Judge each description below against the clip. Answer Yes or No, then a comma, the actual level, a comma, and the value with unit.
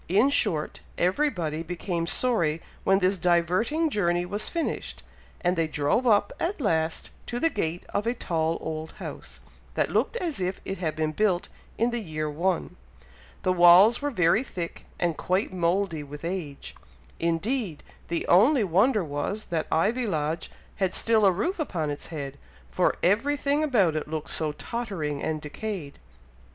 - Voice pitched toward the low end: No, medium, 180 Hz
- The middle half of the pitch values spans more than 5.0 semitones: Yes, wide, 5.4 semitones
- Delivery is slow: No, average, 165 wpm